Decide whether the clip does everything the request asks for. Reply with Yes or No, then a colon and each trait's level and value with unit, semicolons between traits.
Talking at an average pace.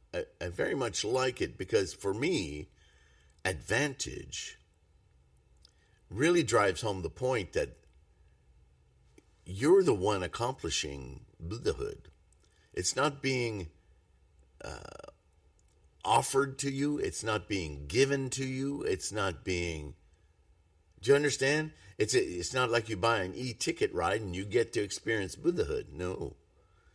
No: slow, 125 wpm